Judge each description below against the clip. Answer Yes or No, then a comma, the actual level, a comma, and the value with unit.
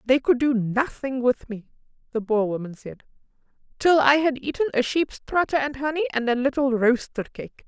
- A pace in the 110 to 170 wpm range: No, average, 190 wpm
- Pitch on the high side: Yes, very high, 260 Hz